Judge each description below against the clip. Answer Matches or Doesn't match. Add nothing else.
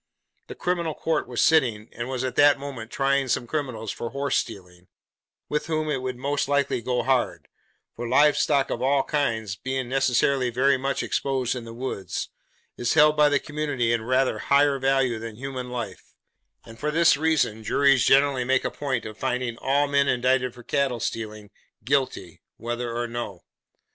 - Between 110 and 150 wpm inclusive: Doesn't match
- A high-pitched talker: Doesn't match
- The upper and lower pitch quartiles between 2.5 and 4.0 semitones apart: Matches